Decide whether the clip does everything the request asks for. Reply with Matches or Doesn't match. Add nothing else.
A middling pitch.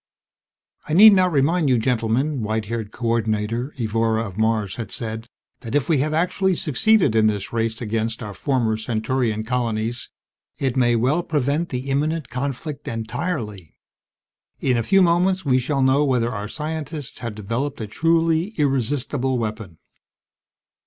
Doesn't match